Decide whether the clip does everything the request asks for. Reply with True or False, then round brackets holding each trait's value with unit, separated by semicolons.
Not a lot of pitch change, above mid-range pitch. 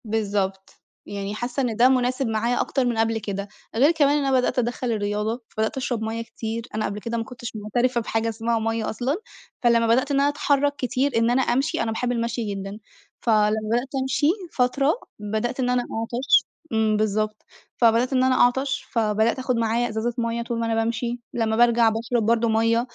True (2.2 semitones; 230 Hz)